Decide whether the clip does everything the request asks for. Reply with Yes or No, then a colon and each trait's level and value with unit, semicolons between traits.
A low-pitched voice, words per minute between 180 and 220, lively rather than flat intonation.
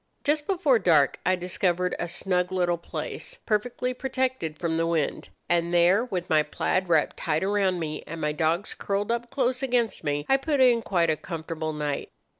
No: medium, 180 Hz; average, 185 wpm; wide, 6.6 semitones